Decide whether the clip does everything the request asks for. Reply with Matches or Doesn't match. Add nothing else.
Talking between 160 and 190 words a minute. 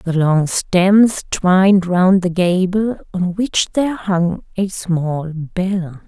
Doesn't match